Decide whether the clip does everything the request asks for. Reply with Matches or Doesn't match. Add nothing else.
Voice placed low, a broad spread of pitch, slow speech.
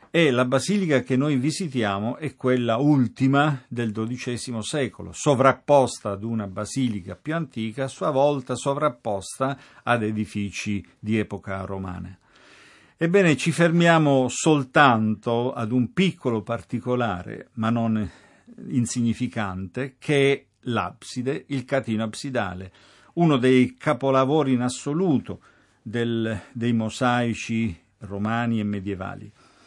Doesn't match